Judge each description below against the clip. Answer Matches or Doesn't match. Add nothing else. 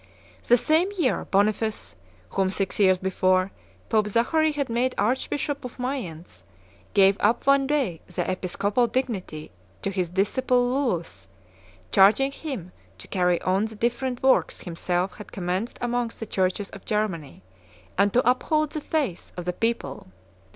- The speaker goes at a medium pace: Matches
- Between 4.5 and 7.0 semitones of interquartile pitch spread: Matches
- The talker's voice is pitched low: Doesn't match